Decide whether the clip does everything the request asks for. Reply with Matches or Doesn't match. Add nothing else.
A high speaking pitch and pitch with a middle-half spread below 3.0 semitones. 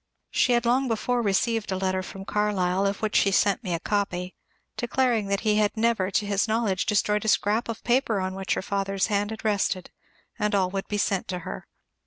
Matches